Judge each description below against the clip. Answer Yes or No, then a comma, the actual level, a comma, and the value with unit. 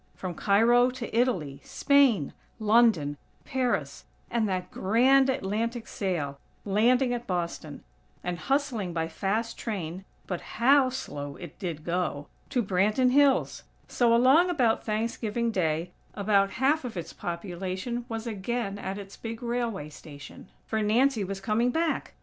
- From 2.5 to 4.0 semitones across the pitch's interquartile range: No, average, 5.1 semitones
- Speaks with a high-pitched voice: Yes, high, 215 Hz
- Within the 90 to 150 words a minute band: Yes, average, 140 wpm